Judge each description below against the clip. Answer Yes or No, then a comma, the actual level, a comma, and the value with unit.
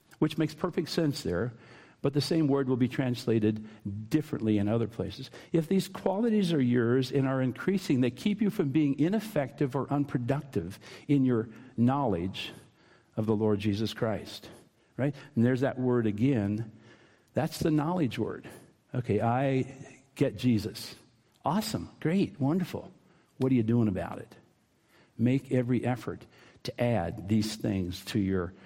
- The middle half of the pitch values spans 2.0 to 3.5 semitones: No, average, 4.7 semitones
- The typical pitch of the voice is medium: No, low, 125 Hz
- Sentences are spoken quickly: No, average, 150 wpm